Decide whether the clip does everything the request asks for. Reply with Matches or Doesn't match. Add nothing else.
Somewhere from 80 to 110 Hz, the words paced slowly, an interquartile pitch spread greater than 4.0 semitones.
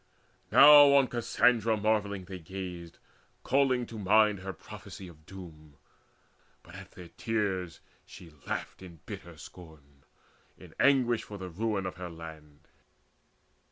Matches